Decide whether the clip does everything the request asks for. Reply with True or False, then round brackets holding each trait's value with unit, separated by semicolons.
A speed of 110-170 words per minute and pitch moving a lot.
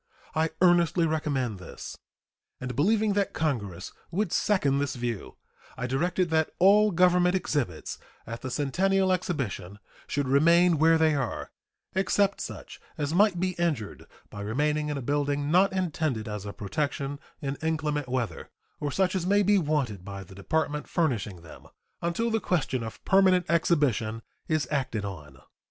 True (155 wpm; 6.4 semitones)